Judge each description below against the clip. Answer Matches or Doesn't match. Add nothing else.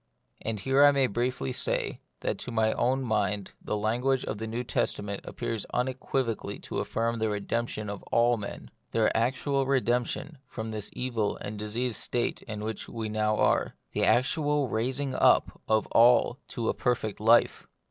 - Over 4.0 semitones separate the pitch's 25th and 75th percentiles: Doesn't match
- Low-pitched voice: Matches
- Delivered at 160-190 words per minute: Matches